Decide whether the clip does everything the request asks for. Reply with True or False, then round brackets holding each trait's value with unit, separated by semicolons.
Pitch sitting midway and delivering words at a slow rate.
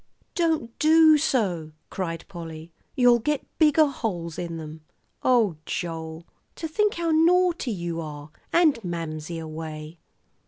True (180 Hz; 125 wpm)